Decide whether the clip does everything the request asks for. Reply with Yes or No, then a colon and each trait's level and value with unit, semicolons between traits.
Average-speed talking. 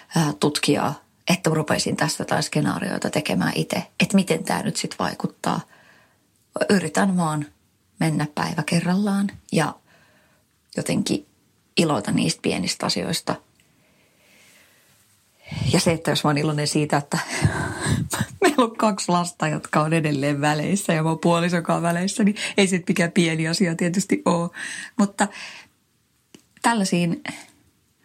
Yes: average, 120 wpm